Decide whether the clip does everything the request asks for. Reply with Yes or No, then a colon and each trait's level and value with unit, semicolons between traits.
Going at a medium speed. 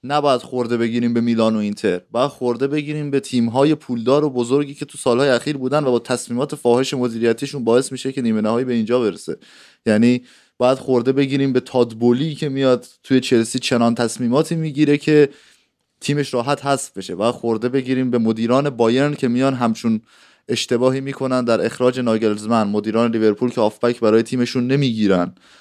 No: fast, 170 wpm